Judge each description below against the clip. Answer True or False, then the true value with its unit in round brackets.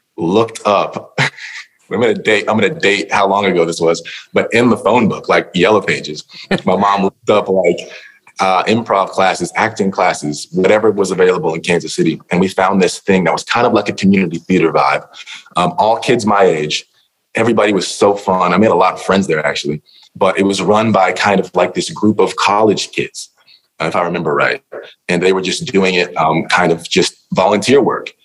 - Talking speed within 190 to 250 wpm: True (205 wpm)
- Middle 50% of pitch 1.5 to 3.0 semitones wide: True (2.7 semitones)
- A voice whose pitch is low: True (95 Hz)